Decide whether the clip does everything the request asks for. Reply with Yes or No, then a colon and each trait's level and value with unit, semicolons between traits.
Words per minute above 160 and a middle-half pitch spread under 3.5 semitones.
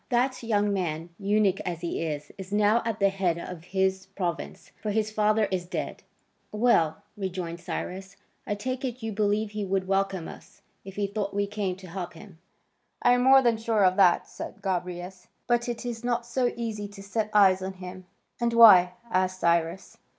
Yes: average, 190 wpm; average, 3.0 semitones